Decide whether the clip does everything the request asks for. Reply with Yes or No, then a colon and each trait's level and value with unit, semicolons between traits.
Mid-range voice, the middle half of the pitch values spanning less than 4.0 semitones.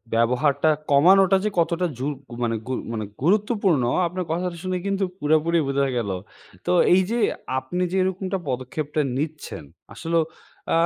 No: medium, 165 Hz; average, 5.1 semitones